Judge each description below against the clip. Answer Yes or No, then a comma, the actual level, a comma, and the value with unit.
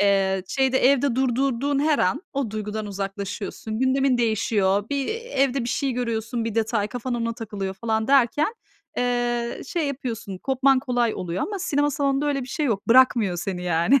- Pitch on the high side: Yes, high, 240 Hz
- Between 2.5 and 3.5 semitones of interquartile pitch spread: No, average, 4.4 semitones